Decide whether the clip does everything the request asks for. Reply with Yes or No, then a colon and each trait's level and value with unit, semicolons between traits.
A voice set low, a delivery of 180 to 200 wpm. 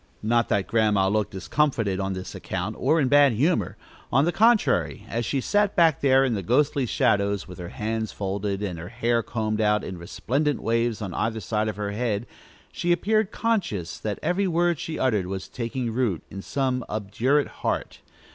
Yes: low, 115 Hz; average, 185 wpm